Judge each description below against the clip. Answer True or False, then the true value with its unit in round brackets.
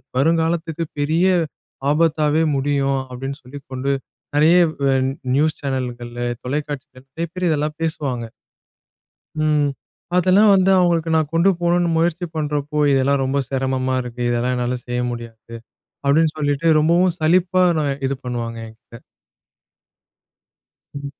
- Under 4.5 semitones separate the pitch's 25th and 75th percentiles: True (3.9 semitones)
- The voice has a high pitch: False (145 Hz)